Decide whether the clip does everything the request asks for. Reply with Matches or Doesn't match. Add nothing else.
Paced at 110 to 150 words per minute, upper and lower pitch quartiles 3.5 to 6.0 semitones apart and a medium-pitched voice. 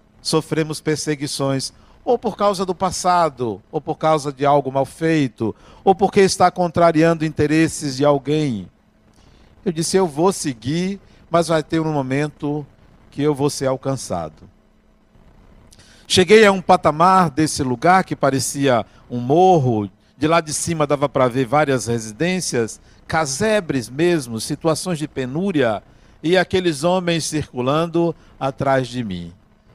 Matches